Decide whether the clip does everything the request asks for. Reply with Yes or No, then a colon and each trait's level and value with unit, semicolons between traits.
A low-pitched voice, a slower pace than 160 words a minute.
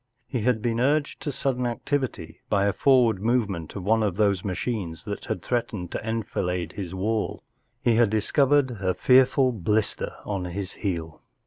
No: low, 110 Hz; average, 175 wpm